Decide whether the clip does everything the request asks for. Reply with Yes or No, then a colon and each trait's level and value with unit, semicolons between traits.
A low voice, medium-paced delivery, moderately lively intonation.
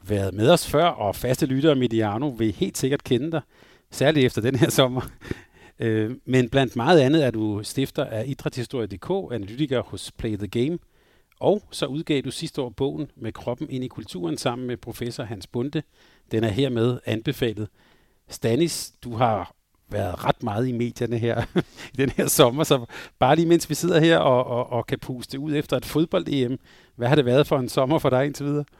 Yes: low, 130 Hz; average, 195 wpm; average, 4.1 semitones